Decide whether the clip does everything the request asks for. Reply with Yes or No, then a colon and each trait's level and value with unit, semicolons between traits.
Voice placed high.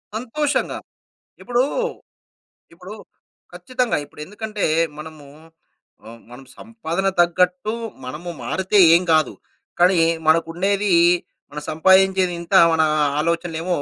No: medium, 180 Hz